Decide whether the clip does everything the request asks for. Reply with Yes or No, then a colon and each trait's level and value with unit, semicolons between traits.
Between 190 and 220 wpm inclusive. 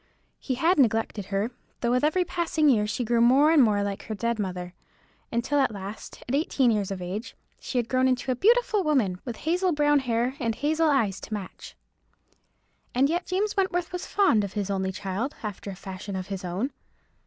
Yes: average, 200 wpm